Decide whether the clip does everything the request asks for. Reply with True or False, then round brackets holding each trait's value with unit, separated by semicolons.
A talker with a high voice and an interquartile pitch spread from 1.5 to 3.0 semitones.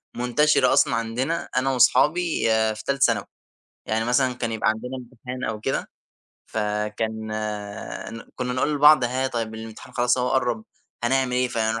False (125 Hz; 2.6 semitones)